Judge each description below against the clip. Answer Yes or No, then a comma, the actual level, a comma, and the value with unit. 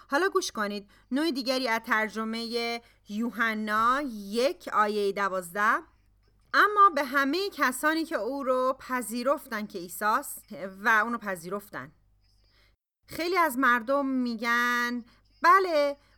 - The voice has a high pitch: Yes, high, 240 Hz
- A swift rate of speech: No, average, 110 wpm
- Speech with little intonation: No, average, 5.2 semitones